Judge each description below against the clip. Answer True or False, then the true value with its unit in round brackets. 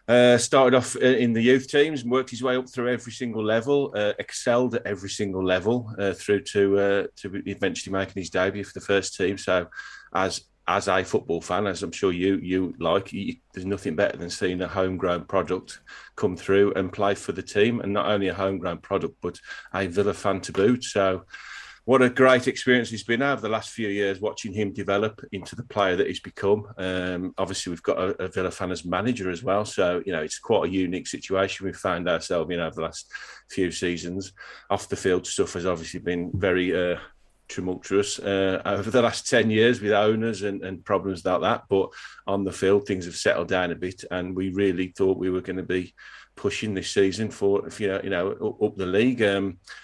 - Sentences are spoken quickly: True (220 wpm)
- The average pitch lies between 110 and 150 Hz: False (100 Hz)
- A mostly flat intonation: False (3.0 semitones)